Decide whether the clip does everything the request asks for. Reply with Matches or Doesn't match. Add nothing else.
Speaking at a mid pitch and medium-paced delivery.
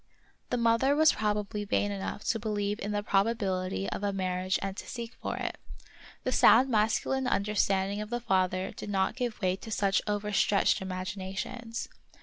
Doesn't match